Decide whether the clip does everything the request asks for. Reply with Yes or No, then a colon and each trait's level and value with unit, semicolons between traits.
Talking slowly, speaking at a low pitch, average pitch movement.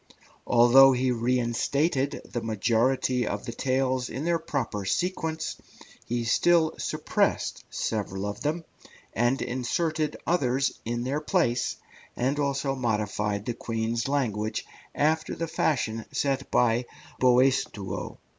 Yes: slow, 120 wpm; low, 125 Hz; average, 3.4 semitones